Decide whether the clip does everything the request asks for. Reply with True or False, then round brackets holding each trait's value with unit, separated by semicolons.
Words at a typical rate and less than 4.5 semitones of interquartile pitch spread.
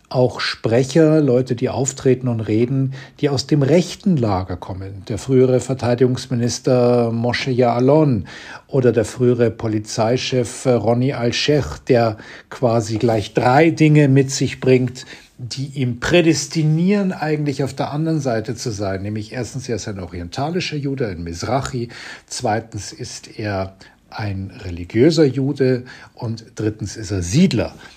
True (135 wpm; 3.5 semitones)